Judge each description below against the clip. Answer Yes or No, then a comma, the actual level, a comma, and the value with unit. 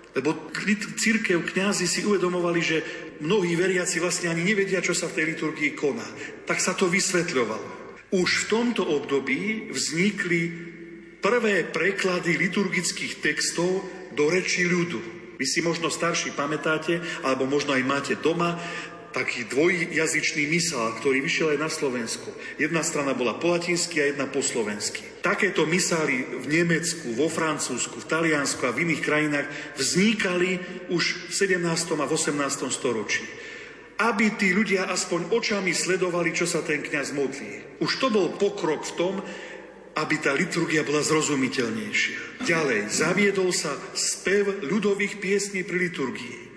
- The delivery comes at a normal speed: Yes, average, 140 wpm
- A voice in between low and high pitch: Yes, medium, 175 Hz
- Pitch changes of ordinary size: Yes, average, 3.2 semitones